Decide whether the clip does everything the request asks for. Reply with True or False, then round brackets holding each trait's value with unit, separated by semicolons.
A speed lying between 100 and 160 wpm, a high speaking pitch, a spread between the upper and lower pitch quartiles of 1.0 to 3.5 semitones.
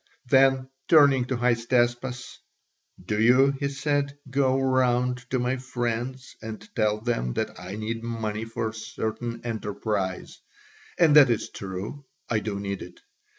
False (145 wpm; 120 Hz; 3.2 semitones)